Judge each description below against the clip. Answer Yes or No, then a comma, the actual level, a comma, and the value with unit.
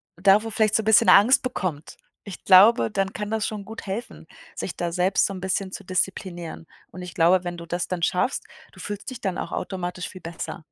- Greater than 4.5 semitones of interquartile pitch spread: No, average, 2.8 semitones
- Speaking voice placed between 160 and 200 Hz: Yes, high, 190 Hz